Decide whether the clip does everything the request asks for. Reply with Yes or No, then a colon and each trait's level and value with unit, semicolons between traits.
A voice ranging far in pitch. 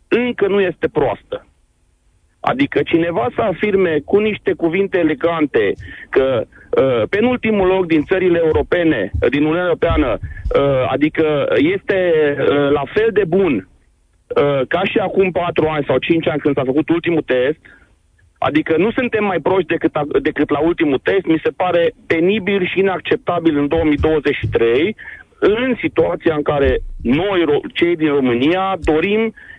Yes: wide, 5.7 semitones